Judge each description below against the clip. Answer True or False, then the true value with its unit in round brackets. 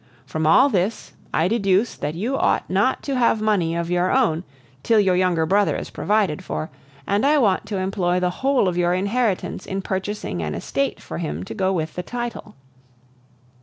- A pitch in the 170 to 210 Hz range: True (190 Hz)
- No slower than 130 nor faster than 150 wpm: False (190 wpm)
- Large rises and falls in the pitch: False (3.7 semitones)